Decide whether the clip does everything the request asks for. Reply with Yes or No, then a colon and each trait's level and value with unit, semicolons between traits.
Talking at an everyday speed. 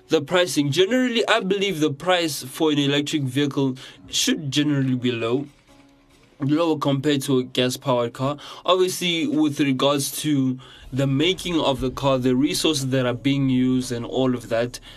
Yes: average, 165 wpm